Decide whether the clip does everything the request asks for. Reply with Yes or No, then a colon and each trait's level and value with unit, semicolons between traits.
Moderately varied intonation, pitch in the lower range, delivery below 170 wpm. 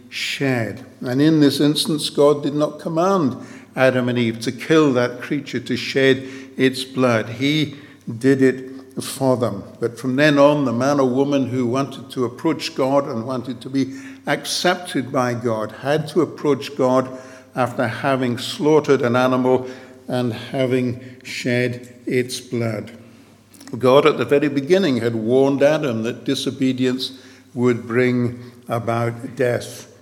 No: narrow, 2.1 semitones; low, 130 Hz; average, 145 wpm